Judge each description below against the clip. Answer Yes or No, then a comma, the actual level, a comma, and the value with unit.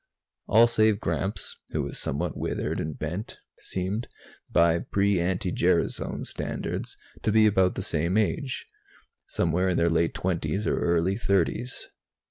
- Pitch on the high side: No, very low, 95 Hz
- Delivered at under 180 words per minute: Yes, average, 140 wpm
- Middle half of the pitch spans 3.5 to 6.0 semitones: Yes, average, 4.0 semitones